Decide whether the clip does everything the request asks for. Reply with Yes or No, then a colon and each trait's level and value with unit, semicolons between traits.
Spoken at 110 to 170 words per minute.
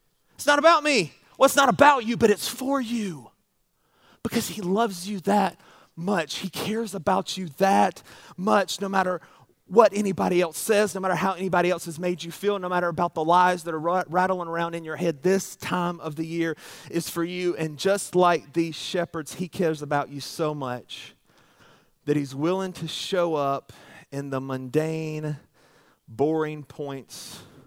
No: average, 180 wpm